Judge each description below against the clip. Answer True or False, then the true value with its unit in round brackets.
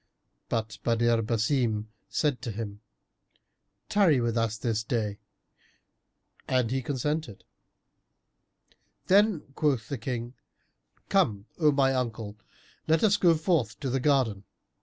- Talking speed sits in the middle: False (115 wpm)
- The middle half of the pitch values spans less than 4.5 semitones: False (4.8 semitones)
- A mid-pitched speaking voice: False (125 Hz)